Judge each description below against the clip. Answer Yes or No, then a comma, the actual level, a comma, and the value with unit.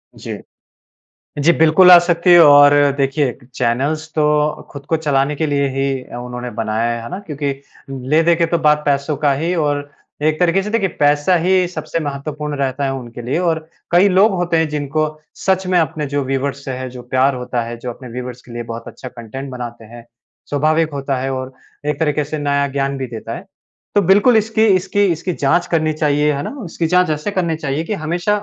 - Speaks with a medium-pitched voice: Yes, medium, 150 Hz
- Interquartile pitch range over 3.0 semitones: Yes, average, 3.7 semitones